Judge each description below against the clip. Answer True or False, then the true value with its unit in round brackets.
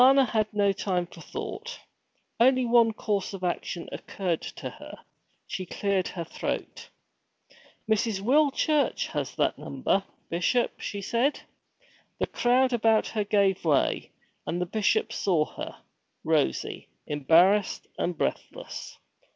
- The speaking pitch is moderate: False (205 Hz)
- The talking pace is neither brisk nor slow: False (130 wpm)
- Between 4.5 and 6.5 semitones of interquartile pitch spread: True (4.8 semitones)